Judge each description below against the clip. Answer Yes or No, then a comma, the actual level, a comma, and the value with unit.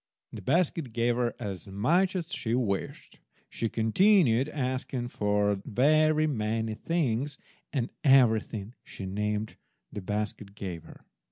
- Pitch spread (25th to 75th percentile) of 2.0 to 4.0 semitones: No, wide, 5.5 semitones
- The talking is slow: Yes, slow, 125 wpm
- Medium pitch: No, low, 115 Hz